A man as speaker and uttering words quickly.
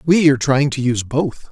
Yes: male; fast, 235 wpm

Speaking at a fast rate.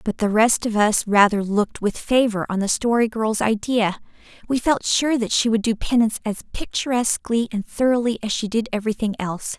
No: average, 195 wpm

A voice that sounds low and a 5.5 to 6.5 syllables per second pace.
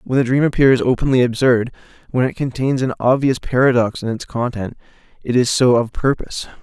Yes: low, 125 Hz; 5.6 syllables/s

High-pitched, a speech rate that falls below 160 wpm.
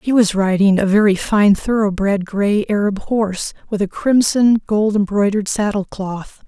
Yes: high, 205 Hz; average, 150 wpm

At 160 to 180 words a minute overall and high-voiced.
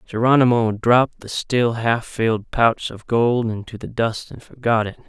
No: average, 175 wpm; low, 115 Hz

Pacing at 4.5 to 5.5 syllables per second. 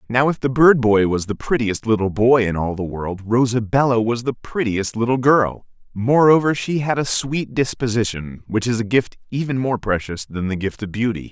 Yes: 5.0 syllables/s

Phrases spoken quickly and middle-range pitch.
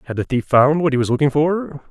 Yes: fast, 285 wpm; medium, 145 Hz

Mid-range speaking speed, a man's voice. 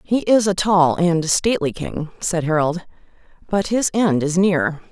No: average, 170 wpm; female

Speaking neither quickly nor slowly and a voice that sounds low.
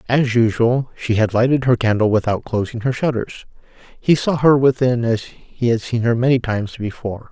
Yes: average, 190 wpm; low, 120 Hz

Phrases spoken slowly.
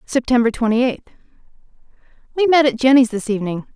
Yes: slow, 130 wpm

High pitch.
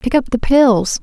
Yes: very high, 250 Hz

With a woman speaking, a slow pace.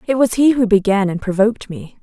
No: female; fast, 235 wpm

